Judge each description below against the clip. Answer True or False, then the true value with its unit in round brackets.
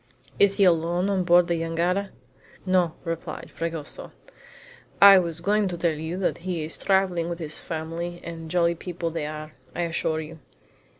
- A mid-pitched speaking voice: True (170 Hz)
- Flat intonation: True (1.9 semitones)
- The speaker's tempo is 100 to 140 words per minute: False (175 wpm)